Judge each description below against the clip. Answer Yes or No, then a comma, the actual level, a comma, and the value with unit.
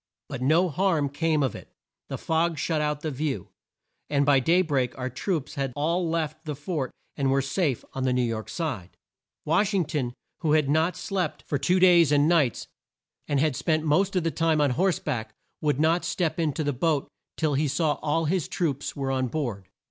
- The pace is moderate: No, fast, 215 wpm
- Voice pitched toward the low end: No, medium, 150 Hz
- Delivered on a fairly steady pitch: No, average, 3.3 semitones